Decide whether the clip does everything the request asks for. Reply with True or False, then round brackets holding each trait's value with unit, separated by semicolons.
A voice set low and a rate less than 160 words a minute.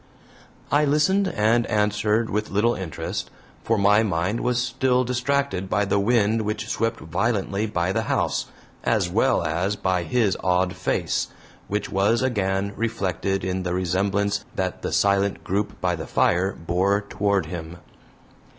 True (100 Hz; 150 wpm)